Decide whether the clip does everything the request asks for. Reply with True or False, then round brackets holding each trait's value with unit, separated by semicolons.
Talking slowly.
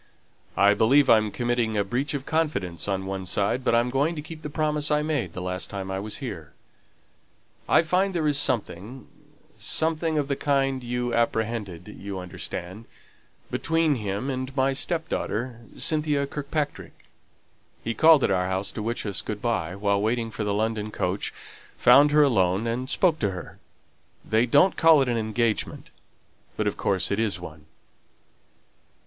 False (170 wpm)